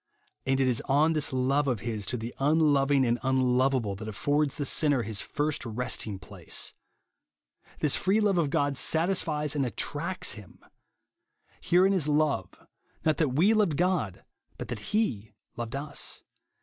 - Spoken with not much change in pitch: No, average, 4.5 semitones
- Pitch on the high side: No, medium, 140 Hz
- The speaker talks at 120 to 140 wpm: No, average, 160 wpm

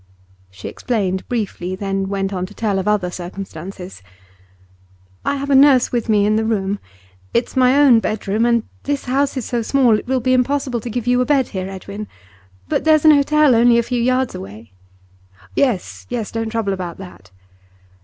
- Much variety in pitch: No, average, 4.7 semitones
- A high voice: Yes, high, 225 Hz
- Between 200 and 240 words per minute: No, average, 185 wpm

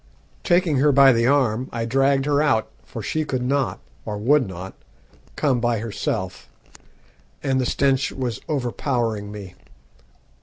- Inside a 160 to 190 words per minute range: No, average, 145 wpm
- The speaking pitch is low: Yes, low, 130 Hz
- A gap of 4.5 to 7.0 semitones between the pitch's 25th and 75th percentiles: No, average, 3.5 semitones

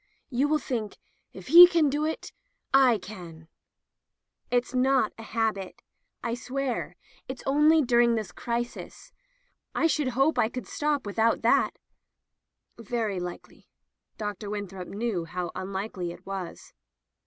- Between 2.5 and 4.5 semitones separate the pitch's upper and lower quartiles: No, wide, 5.5 semitones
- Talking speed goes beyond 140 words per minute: No, slow, 135 wpm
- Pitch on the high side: Yes, high, 230 Hz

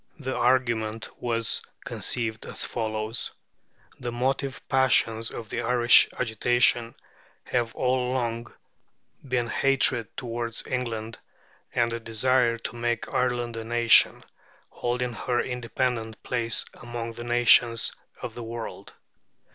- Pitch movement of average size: No, narrow, 1.4 semitones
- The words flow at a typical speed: No, slow, 115 wpm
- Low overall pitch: Yes, low, 120 Hz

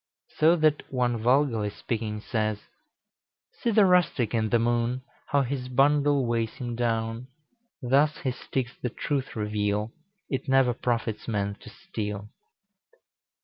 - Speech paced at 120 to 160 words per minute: Yes, slow, 135 wpm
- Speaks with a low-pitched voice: Yes, low, 120 Hz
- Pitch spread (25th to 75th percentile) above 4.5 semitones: No, average, 3.6 semitones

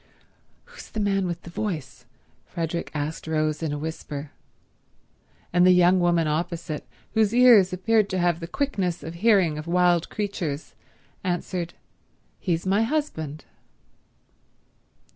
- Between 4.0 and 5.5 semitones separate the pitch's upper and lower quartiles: No, average, 3.6 semitones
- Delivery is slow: Yes, slow, 130 wpm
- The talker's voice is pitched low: No, medium, 175 Hz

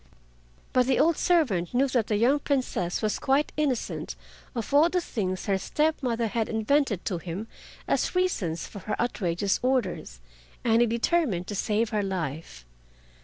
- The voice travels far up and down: Yes, wide, 6.1 semitones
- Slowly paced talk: No, average, 165 wpm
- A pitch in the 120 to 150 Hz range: No, high, 230 Hz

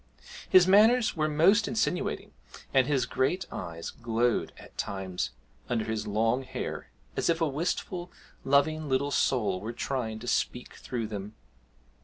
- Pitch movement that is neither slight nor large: No, wide, 6.1 semitones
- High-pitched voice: No, low, 130 Hz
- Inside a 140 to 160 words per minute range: Yes, average, 145 wpm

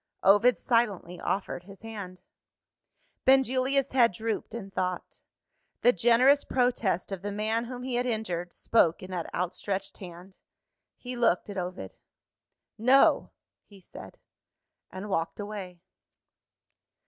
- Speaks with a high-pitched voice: Yes, high, 205 Hz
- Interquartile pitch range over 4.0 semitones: Yes, average, 4.8 semitones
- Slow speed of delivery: Yes, slow, 125 wpm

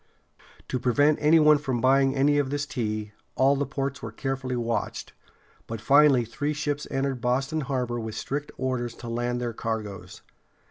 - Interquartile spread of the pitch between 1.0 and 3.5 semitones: Yes, average, 3.1 semitones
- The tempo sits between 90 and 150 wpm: No, average, 170 wpm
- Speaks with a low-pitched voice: Yes, low, 130 Hz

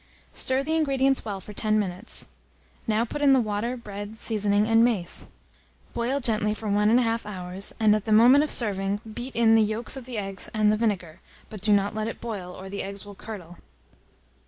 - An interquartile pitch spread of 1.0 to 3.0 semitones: Yes, narrow, 2.5 semitones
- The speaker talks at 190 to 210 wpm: Yes, fast, 205 wpm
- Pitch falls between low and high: No, high, 215 Hz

